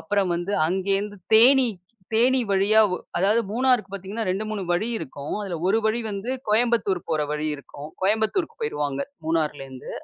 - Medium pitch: No, high, 200 Hz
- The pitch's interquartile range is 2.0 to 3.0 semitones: No, average, 4.1 semitones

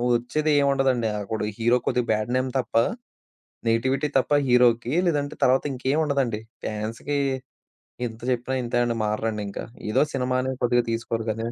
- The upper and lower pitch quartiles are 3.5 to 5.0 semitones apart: No, average, 2.9 semitones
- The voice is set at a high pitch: No, low, 125 Hz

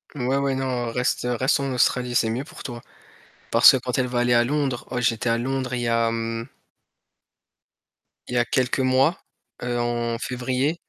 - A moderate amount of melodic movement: No, narrow, 1.7 semitones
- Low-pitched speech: Yes, low, 125 Hz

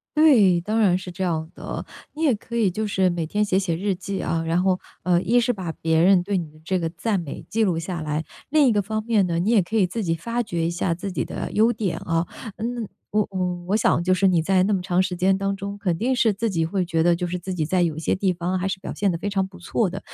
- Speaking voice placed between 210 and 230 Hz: No, medium, 185 Hz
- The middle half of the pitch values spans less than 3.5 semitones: Yes, average, 3.1 semitones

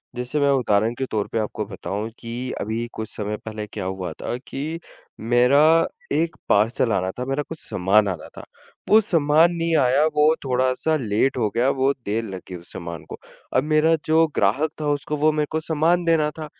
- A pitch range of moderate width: No, wide, 6.2 semitones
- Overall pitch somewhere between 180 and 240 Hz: No, low, 130 Hz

